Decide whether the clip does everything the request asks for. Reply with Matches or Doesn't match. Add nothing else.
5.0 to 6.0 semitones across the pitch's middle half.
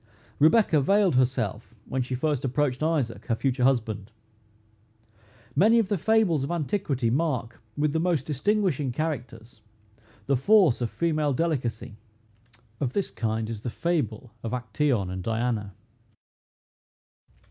Matches